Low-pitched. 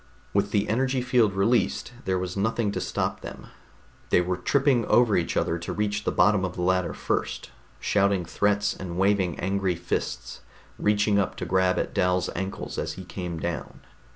Yes: very low, 95 Hz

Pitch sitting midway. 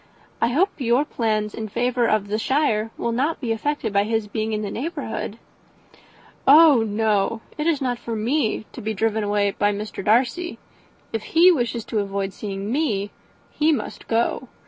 No: high, 225 Hz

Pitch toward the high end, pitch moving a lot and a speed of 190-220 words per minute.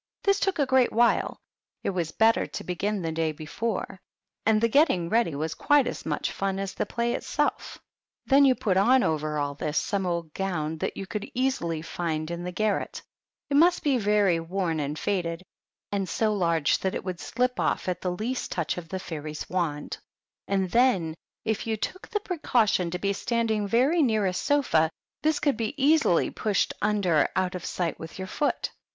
Yes: high, 195 Hz; wide, 5.7 semitones; average, 195 wpm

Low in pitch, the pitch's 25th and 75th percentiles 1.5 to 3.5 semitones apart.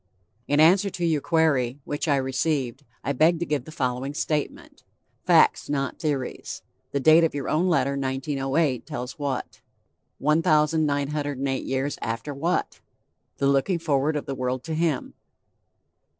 No: medium, 145 Hz; average, 2.8 semitones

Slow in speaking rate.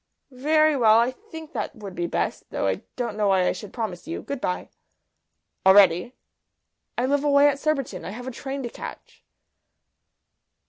No: average, 175 wpm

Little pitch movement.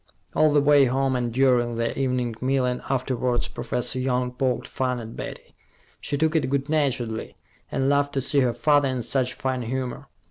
Yes: narrow, 1.8 semitones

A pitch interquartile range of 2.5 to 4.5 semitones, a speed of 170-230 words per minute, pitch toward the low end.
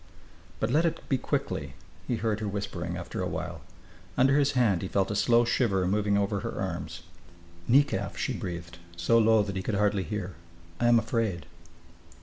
Yes: average, 3.7 semitones; average, 180 wpm; low, 105 Hz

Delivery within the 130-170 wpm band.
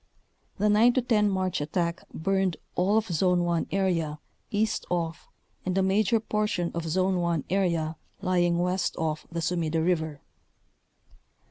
Yes: average, 145 wpm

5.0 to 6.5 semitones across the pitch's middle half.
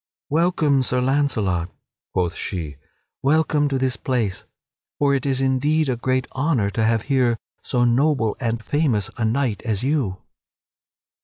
No: average, 4.1 semitones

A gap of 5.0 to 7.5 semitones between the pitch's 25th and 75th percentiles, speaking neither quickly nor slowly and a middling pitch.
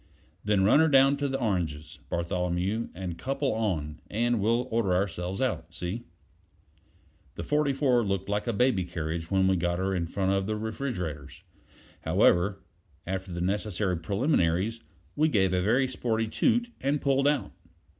No: wide, 5.6 semitones; average, 155 wpm; low, 100 Hz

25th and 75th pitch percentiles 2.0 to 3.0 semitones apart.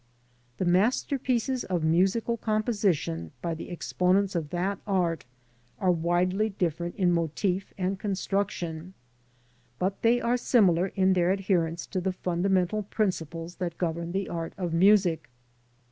Yes: average, 2.7 semitones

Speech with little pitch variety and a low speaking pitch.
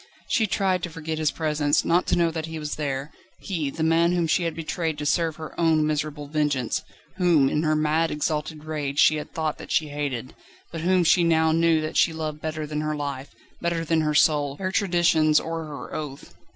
No: narrow, 1.7 semitones; medium, 155 Hz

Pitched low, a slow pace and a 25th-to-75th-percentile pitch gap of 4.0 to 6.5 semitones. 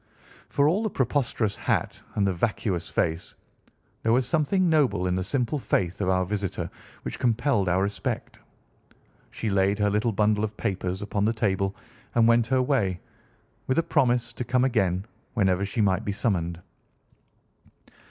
No: low, 105 Hz; average, 160 wpm; average, 4.5 semitones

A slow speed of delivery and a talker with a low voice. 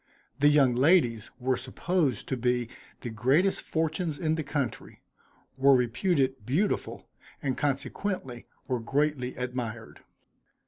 Yes: slow, 120 wpm; low, 130 Hz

